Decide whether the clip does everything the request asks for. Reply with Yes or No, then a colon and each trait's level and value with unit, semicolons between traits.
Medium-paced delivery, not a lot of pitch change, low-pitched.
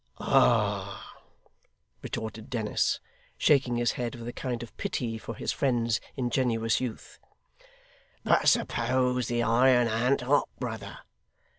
No: slow, 120 wpm; narrow, 1.6 semitones; low, 120 Hz